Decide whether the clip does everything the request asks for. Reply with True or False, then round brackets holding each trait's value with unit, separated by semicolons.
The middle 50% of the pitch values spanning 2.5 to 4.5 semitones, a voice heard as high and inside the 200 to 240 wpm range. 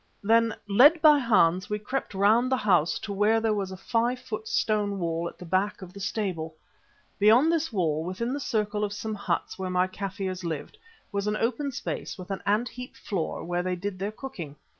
True (3.7 semitones; 205 Hz; 205 wpm)